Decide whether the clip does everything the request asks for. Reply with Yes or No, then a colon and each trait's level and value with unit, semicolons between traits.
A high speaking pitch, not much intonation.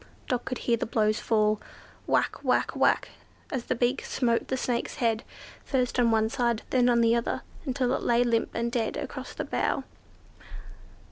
Yes: high, 235 Hz; narrow, 1.5 semitones